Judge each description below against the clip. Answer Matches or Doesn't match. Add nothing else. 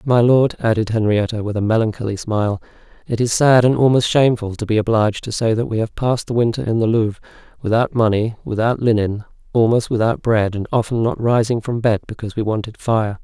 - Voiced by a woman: Doesn't match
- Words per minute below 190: Doesn't match